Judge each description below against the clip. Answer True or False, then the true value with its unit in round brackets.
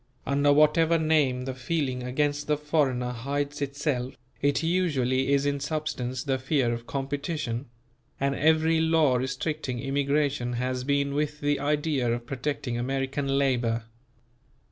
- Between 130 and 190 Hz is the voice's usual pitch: True (140 Hz)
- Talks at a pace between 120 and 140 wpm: True (135 wpm)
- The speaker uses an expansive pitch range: False (2.6 semitones)